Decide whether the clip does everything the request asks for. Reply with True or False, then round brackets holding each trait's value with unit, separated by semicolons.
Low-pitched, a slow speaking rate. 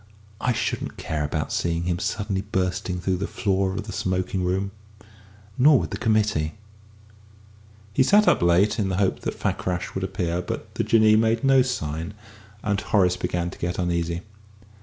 False (95 Hz; 170 wpm)